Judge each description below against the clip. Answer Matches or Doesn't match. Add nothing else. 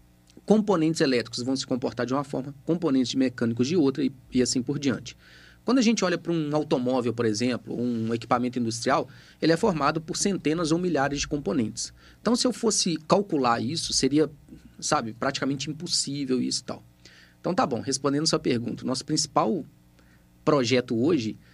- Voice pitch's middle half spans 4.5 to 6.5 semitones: Matches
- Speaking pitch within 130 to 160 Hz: Matches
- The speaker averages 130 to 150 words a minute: Doesn't match